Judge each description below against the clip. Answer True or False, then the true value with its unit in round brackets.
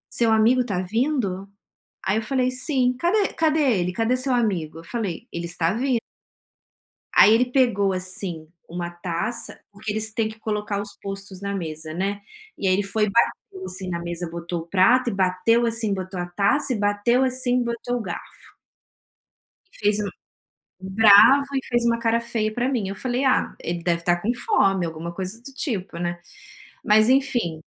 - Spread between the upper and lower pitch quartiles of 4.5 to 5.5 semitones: True (4.8 semitones)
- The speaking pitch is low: False (210 Hz)